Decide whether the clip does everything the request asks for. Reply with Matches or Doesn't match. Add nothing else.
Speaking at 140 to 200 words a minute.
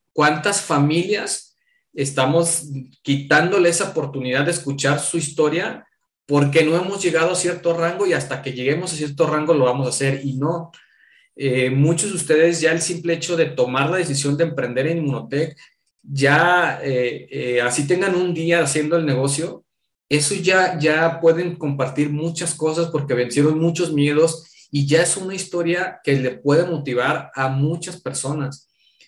Matches